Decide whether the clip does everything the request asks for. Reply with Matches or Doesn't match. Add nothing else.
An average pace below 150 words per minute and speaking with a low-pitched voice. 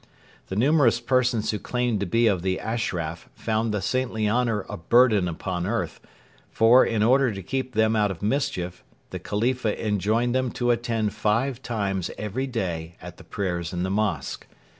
Doesn't match